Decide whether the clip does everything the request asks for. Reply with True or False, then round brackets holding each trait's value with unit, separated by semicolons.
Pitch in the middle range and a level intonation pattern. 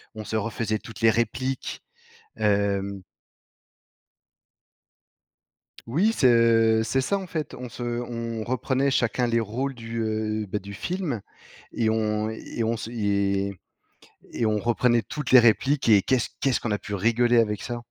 False (115 Hz; 2.3 semitones)